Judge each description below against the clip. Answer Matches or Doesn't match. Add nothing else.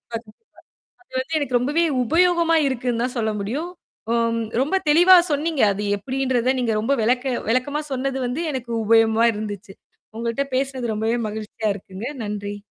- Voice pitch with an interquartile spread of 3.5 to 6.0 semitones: Matches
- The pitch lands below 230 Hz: Doesn't match